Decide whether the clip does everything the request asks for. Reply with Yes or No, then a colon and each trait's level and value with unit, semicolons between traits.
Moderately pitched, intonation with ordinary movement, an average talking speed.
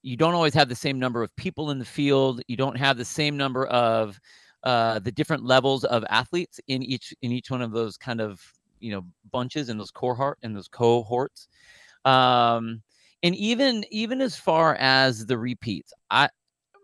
No: low, 130 Hz; average, 3.8 semitones; average, 190 wpm